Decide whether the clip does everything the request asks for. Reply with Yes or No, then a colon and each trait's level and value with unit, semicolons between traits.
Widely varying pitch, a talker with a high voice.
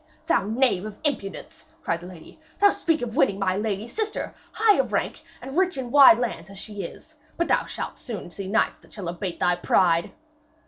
Yes: wide, 7.0 semitones; high, 215 Hz